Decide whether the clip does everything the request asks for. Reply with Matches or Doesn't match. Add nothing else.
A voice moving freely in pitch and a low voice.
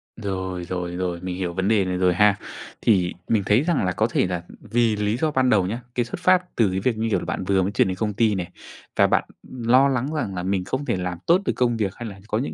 Doesn't match